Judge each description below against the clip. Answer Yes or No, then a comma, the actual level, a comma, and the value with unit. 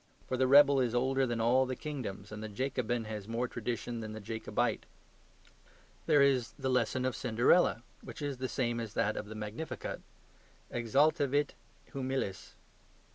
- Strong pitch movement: No, average, 3.2 semitones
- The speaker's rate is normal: Yes, average, 160 wpm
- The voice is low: Yes, low, 120 Hz